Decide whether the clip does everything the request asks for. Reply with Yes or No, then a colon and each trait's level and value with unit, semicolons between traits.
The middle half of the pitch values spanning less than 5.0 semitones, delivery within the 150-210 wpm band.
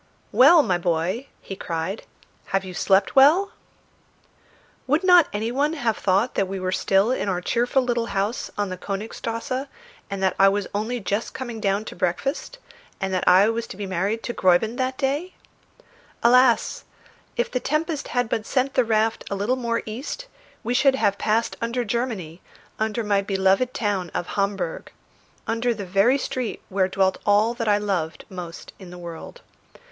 Yes: average, 4.5 semitones; average, 175 wpm